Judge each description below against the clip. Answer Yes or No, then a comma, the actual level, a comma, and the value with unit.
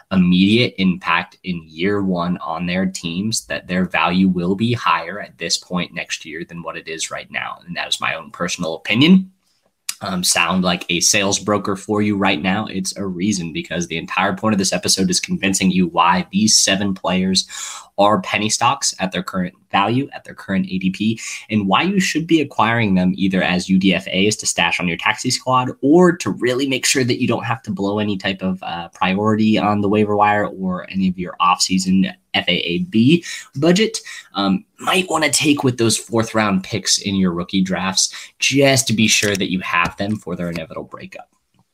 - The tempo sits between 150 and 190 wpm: No, average, 200 wpm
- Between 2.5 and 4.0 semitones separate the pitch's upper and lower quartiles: No, average, 4.9 semitones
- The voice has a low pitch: Yes, low, 100 Hz